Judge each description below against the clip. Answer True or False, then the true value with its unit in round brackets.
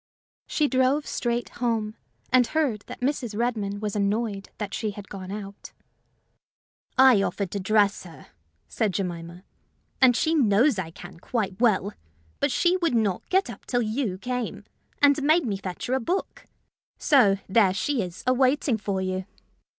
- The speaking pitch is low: False (220 Hz)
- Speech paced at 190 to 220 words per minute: False (165 wpm)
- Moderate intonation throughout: True (4.6 semitones)